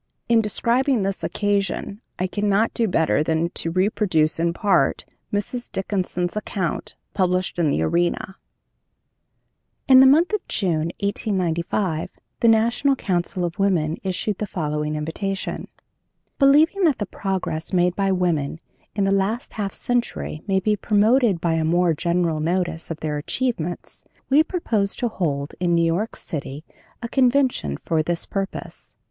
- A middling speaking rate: Yes, average, 145 wpm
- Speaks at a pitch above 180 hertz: Yes, high, 190 Hz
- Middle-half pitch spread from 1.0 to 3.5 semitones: No, average, 4.3 semitones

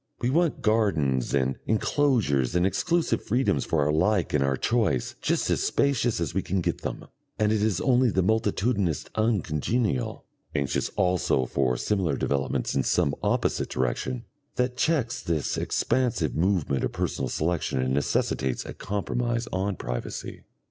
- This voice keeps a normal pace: Yes, average, 150 wpm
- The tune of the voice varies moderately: No, wide, 8.7 semitones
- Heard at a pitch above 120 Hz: No, very low, 95 Hz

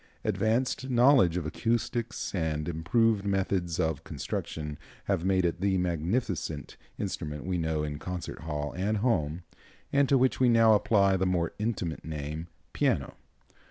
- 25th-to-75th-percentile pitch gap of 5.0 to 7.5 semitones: Yes, wide, 5.5 semitones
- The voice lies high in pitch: No, very low, 90 Hz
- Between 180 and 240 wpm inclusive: No, average, 145 wpm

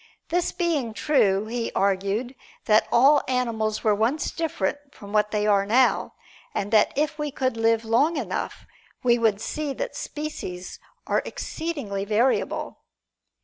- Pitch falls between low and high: No, high, 230 Hz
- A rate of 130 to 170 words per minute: Yes, average, 145 wpm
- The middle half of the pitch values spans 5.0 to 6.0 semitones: Yes, wide, 5.4 semitones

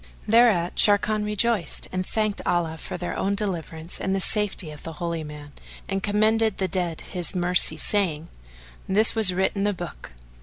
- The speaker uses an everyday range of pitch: Yes, average, 3.7 semitones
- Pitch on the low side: No, high, 190 Hz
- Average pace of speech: Yes, average, 185 wpm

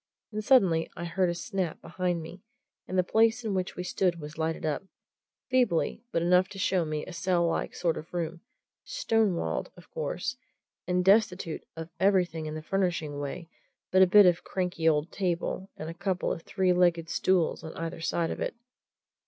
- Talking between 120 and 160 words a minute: No, average, 195 wpm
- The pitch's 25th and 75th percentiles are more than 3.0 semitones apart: No, narrow, 2.4 semitones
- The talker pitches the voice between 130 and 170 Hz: No, medium, 180 Hz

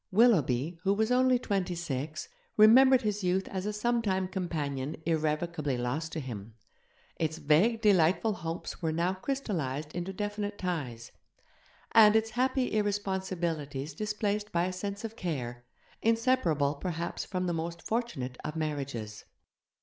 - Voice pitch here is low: No, medium, 180 Hz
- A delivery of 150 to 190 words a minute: No, slow, 135 wpm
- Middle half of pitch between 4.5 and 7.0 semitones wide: Yes, wide, 5.6 semitones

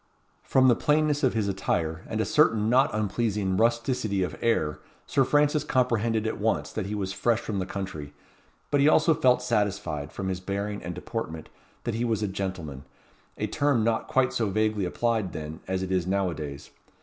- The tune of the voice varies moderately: Yes, average, 4.1 semitones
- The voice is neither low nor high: No, low, 105 Hz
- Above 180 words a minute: Yes, average, 195 wpm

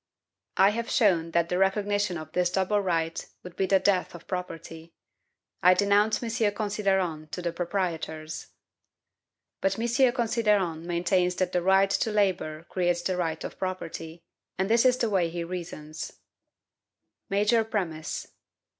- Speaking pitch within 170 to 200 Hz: Yes, medium, 185 Hz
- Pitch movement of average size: Yes, average, 3.4 semitones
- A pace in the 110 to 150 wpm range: Yes, average, 145 wpm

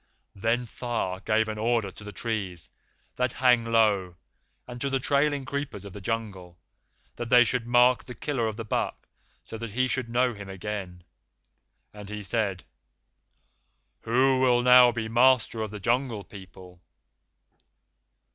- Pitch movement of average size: Yes, average, 3.4 semitones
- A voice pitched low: Yes, low, 115 Hz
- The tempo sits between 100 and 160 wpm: Yes, average, 155 wpm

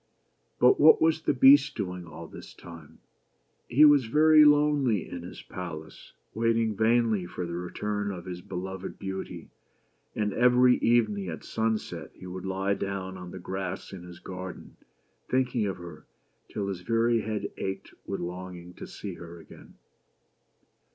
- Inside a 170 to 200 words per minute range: No, average, 155 wpm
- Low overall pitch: Yes, low, 100 Hz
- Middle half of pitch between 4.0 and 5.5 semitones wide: Yes, average, 4.5 semitones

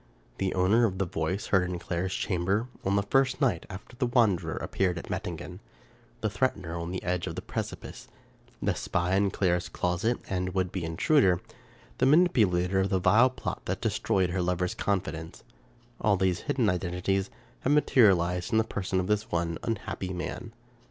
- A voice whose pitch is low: Yes, very low, 95 Hz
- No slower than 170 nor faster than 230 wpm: Yes, average, 180 wpm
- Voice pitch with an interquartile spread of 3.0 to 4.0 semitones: Yes, average, 3.5 semitones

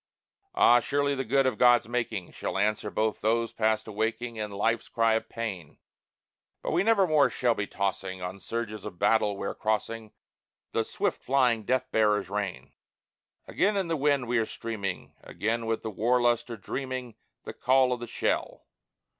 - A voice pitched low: Yes, low, 115 Hz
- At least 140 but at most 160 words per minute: No, average, 170 wpm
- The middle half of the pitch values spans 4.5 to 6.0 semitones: No, average, 2.9 semitones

